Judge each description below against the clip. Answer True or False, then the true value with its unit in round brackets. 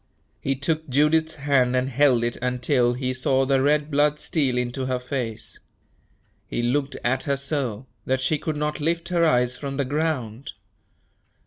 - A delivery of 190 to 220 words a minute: False (165 wpm)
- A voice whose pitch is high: False (135 Hz)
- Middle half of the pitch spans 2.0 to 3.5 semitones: True (3.0 semitones)